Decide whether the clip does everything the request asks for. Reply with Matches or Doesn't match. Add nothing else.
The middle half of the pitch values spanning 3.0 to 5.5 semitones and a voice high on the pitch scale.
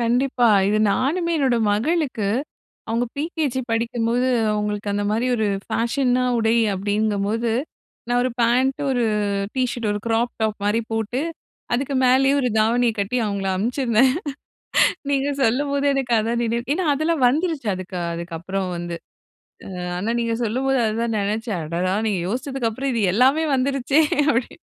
Matches